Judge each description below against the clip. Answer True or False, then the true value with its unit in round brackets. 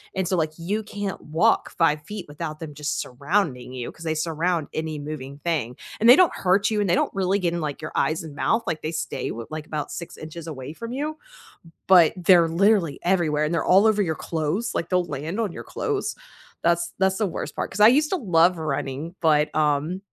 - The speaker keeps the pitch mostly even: False (4.0 semitones)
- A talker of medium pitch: True (170 Hz)